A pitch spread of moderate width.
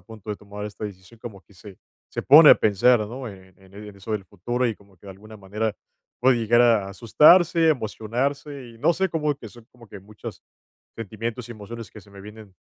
Yes: average, 3.3 semitones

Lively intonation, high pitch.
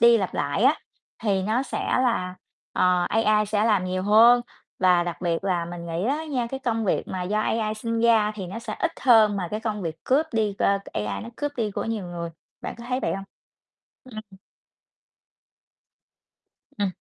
No: average, 4.0 semitones; high, 210 Hz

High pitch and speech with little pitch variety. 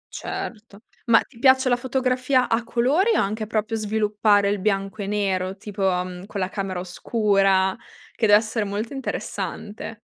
No: high, 210 Hz; average, 3.1 semitones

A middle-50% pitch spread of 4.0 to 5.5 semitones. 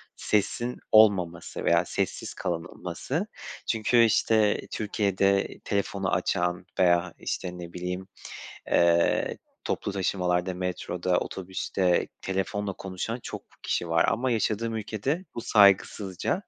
No: average, 3.0 semitones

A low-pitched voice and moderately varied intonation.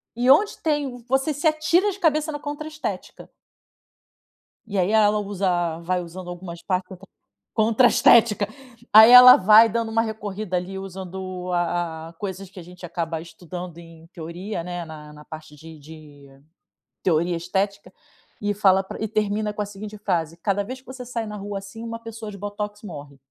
No: high, 195 Hz; average, 4.2 semitones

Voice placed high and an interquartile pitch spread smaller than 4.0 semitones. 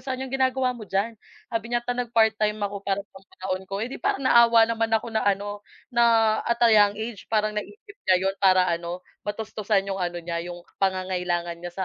Yes: high, 210 Hz; average, 3.5 semitones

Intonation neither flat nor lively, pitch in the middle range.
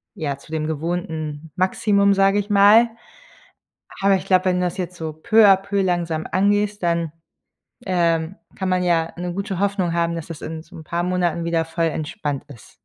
Yes: average, 3.2 semitones; medium, 175 Hz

